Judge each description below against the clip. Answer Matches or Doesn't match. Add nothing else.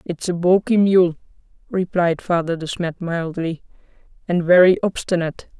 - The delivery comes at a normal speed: Doesn't match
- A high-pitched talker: Doesn't match